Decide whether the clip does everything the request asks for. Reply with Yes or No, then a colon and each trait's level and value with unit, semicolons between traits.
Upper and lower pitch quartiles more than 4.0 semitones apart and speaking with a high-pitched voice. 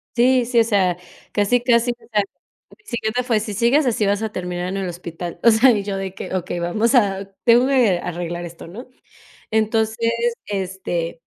Yes: average, 4.5 semitones; high, 210 Hz